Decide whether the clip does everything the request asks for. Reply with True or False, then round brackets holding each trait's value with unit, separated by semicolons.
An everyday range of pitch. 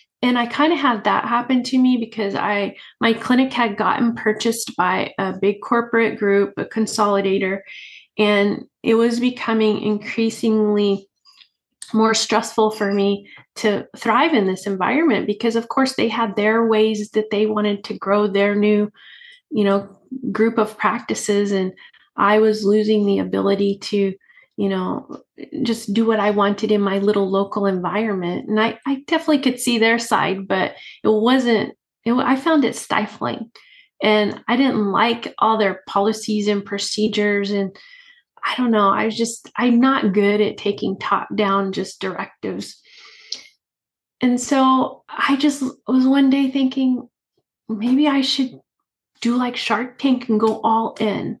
True (3.4 semitones)